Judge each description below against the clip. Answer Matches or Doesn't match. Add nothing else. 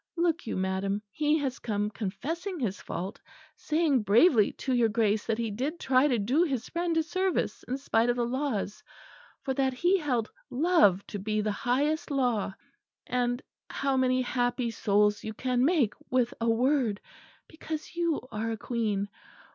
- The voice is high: Matches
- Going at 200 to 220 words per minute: Doesn't match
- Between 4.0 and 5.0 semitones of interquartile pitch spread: Doesn't match